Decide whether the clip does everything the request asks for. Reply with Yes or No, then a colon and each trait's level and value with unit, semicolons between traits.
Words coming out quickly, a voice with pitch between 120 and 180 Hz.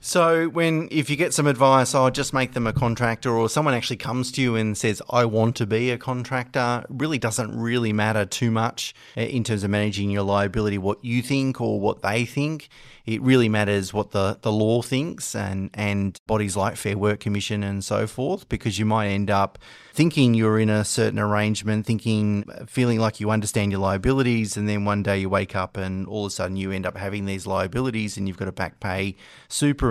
No: fast, 215 wpm; low, 110 Hz